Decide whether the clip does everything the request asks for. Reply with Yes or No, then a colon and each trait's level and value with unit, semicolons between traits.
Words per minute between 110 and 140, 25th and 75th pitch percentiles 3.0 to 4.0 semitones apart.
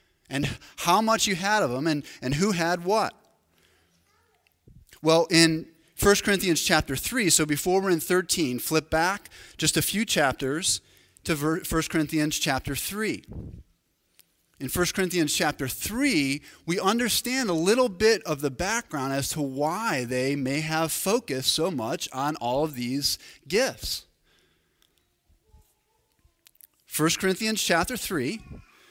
No: slow, 135 wpm; wide, 5.4 semitones